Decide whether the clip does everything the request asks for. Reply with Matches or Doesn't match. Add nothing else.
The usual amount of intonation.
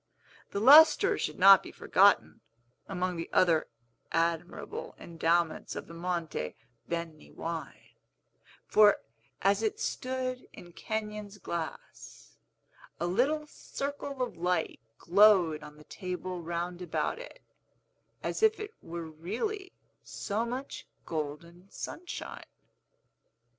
Doesn't match